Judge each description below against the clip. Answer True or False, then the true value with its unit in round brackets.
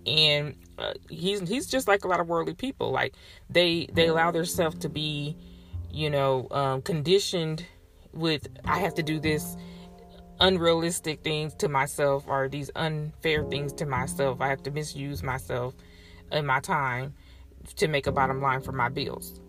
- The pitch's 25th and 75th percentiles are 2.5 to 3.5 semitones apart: False (4.0 semitones)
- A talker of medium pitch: True (145 Hz)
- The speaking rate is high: False (165 wpm)